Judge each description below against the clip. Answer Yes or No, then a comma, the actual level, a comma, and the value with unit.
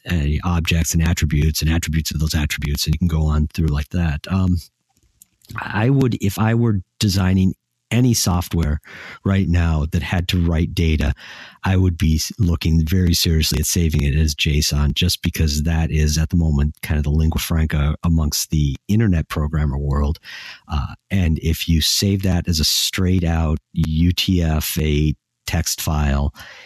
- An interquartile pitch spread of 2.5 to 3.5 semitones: Yes, average, 2.9 semitones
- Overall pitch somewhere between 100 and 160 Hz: No, very low, 80 Hz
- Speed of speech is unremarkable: Yes, average, 165 wpm